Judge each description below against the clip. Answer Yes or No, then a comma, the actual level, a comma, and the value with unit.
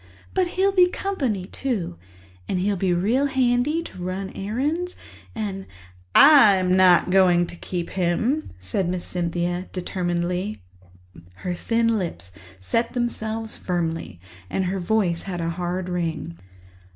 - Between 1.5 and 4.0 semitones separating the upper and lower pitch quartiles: No, average, 4.9 semitones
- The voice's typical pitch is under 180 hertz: No, high, 190 Hz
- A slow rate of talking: Yes, slow, 130 wpm